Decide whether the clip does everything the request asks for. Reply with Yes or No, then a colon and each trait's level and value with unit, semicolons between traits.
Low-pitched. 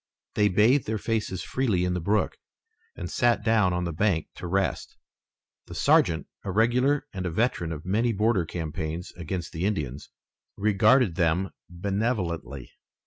Yes: very low, 95 Hz